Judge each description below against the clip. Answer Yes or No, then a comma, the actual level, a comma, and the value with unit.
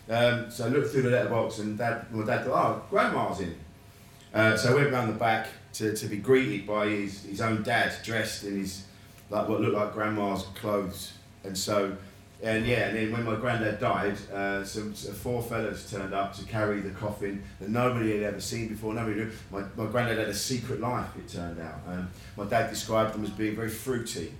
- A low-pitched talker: Yes, low, 105 Hz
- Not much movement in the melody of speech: Yes, narrow, 2.3 semitones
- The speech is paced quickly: Yes, fast, 215 wpm